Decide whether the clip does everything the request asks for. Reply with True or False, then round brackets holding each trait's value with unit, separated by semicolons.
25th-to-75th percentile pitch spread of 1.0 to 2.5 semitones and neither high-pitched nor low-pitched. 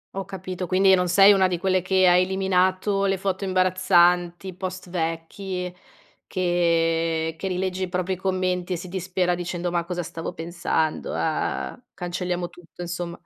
True (1.3 semitones; 180 Hz)